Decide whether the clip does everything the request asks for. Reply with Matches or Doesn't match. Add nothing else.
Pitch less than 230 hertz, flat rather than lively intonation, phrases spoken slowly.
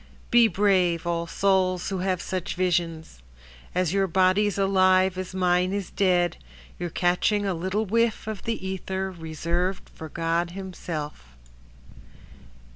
Matches